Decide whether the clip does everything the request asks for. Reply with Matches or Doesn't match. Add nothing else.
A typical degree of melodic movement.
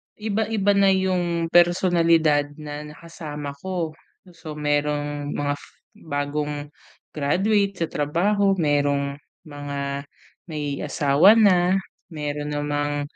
Matches